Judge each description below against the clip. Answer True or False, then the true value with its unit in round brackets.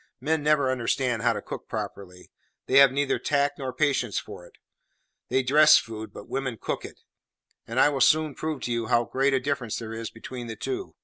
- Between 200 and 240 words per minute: True (205 wpm)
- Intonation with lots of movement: False (3.5 semitones)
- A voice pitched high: False (130 Hz)